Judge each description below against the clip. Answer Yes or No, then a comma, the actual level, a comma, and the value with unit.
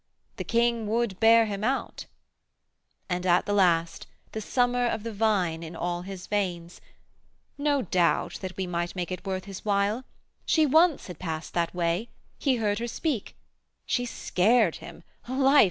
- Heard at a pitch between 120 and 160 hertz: No, high, 205 Hz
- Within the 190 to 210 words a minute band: No, average, 165 wpm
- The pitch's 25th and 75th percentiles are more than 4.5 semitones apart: Yes, average, 5.0 semitones